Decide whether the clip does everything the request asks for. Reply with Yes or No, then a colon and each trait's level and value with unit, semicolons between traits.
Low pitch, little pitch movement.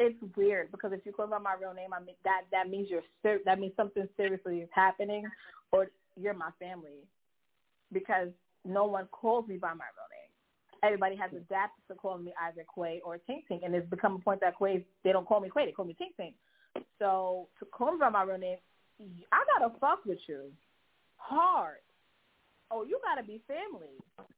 No: high, 190 Hz; narrow, 2.3 semitones